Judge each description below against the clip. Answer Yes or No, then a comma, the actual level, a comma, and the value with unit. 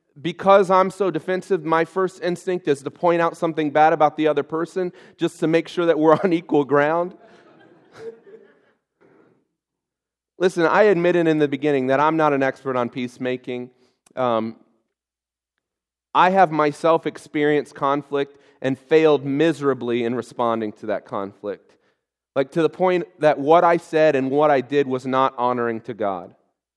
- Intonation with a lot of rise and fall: No, average, 4.3 semitones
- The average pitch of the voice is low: No, medium, 150 Hz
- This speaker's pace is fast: No, average, 155 wpm